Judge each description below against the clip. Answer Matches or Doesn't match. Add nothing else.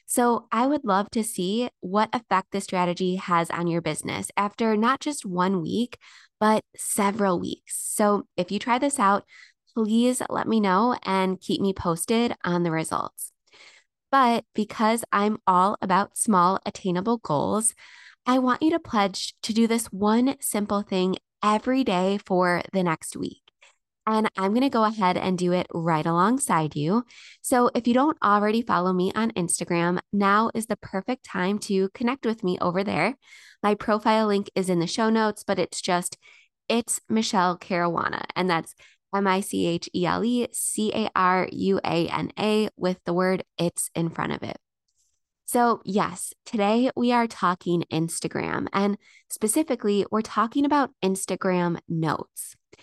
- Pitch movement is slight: Doesn't match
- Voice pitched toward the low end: Doesn't match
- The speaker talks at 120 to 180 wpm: Matches